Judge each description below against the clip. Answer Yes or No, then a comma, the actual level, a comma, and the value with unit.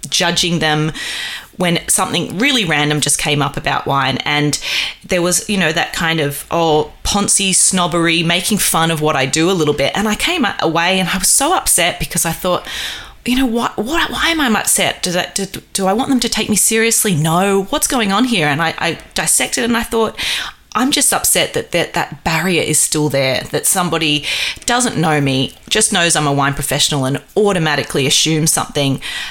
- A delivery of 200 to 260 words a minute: Yes, fast, 205 wpm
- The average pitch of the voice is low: No, medium, 170 Hz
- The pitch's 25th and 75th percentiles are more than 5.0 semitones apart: Yes, wide, 5.5 semitones